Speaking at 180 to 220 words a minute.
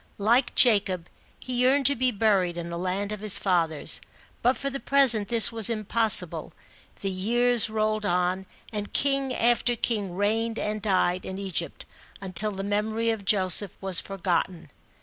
No: average, 160 wpm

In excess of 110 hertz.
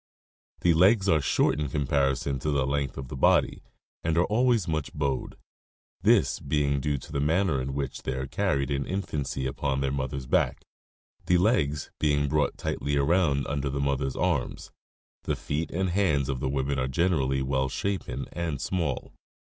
No: very low, 70 Hz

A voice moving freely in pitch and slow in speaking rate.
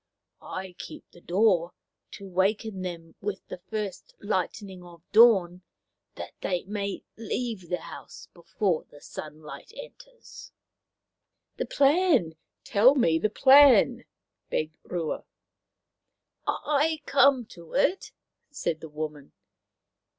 Yes: wide, 5.8 semitones; slow, 120 wpm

